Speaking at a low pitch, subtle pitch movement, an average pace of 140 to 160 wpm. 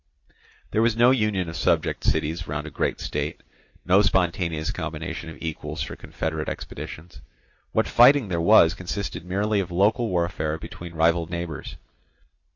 No: very low, 85 Hz; average, 3.9 semitones; average, 150 wpm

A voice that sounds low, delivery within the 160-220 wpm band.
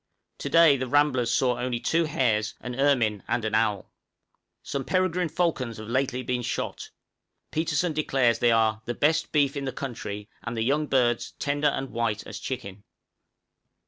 Yes: low, 130 Hz; average, 170 wpm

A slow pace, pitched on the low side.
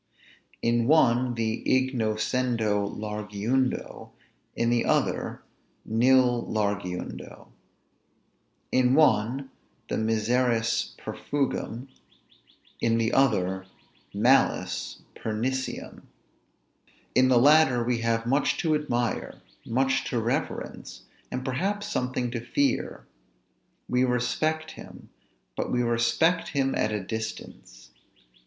Yes: slow, 95 wpm; low, 120 Hz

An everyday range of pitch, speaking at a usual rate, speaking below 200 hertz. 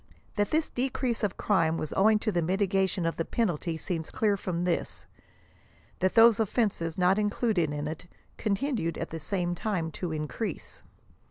Yes: average, 4.5 semitones; average, 175 wpm; high, 190 Hz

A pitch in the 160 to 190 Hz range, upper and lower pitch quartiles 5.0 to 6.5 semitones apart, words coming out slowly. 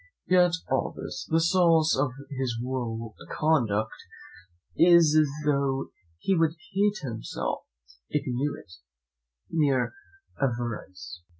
No: medium, 140 Hz; average, 5.3 semitones; slow, 115 wpm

